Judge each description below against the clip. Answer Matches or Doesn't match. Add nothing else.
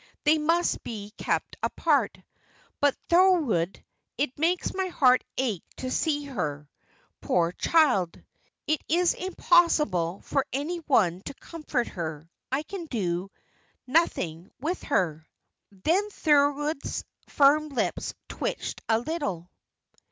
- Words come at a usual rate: Doesn't match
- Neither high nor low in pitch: Doesn't match